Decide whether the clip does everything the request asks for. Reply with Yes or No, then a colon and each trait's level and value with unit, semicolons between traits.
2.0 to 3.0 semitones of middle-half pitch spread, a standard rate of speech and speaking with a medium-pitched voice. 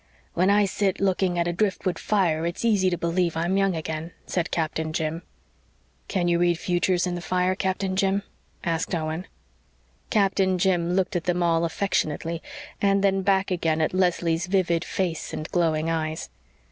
Yes: narrow, 2.4 semitones; average, 170 wpm; medium, 175 Hz